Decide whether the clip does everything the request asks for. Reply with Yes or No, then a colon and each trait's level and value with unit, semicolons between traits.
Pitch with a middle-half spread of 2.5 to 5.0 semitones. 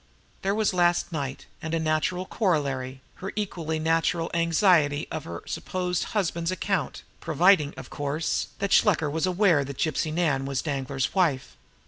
Yes: average, 4.0 semitones